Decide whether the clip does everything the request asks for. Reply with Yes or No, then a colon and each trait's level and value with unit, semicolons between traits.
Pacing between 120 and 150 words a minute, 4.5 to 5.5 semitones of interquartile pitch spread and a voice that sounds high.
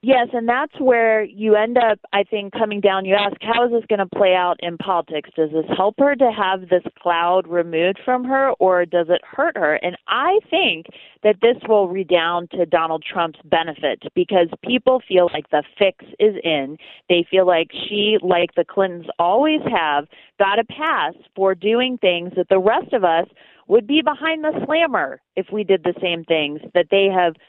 No: average, 200 wpm; average, 4.9 semitones; high, 195 Hz